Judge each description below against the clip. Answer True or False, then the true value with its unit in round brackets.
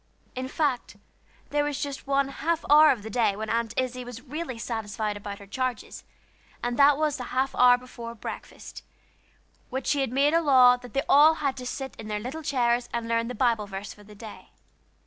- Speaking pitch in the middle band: False (250 Hz)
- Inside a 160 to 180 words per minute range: False (205 wpm)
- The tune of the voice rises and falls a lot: False (3.4 semitones)